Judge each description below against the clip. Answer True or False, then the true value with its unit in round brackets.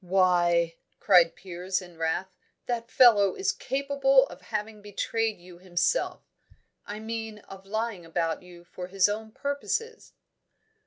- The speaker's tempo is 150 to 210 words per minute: False (140 wpm)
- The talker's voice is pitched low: False (195 Hz)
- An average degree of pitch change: True (4.1 semitones)